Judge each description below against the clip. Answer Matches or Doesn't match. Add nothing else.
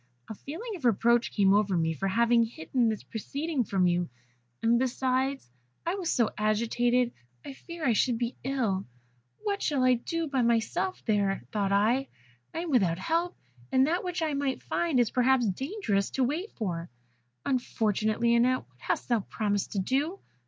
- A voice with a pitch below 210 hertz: Doesn't match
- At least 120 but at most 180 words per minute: Matches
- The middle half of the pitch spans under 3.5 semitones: Doesn't match